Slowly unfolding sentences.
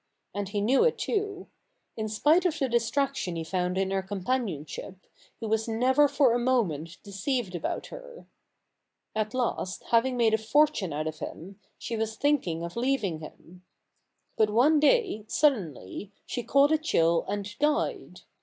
No: average, 160 wpm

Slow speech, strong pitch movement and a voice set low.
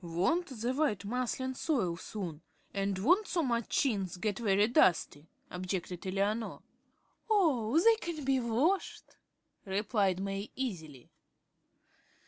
No: slow, 115 wpm; wide, 5.7 semitones; high, 215 Hz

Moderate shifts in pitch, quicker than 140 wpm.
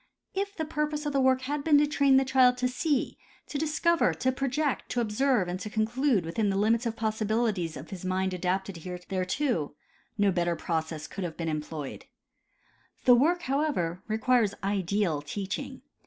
No: wide, 7.0 semitones; average, 175 wpm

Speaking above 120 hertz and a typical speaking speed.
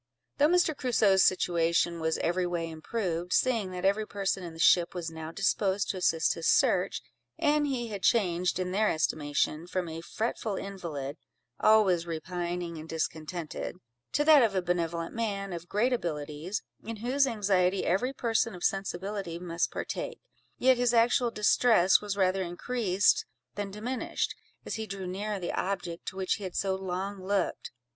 Yes: high, 190 Hz; average, 165 wpm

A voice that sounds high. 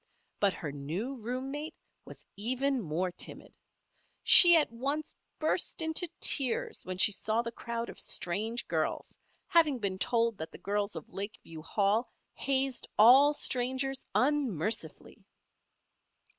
Yes: high, 235 Hz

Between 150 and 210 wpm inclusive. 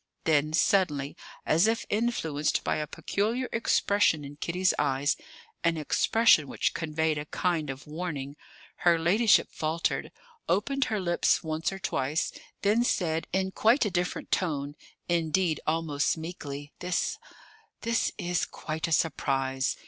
No: slow, 135 wpm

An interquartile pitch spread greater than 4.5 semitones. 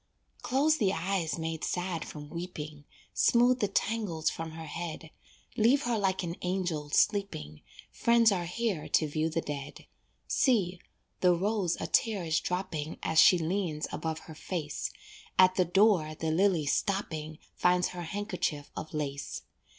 No: average, 4.0 semitones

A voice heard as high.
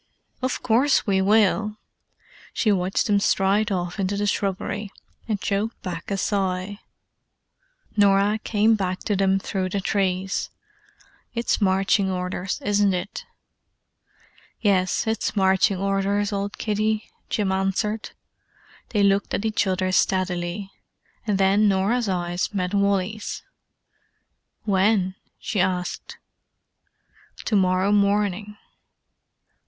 Yes: high, 200 Hz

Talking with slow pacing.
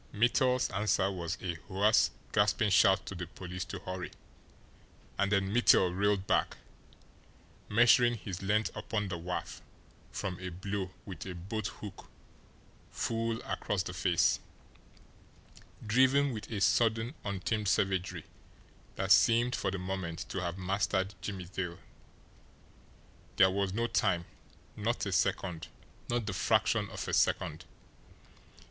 Yes: slow, 130 wpm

